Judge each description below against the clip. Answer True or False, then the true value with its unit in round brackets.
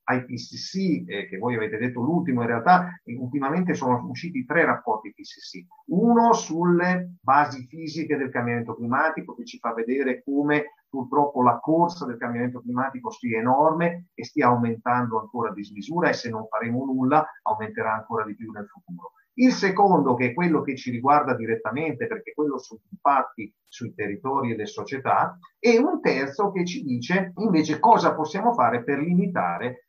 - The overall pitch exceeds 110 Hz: True (140 Hz)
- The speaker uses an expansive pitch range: True (6.6 semitones)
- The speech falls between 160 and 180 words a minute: True (170 wpm)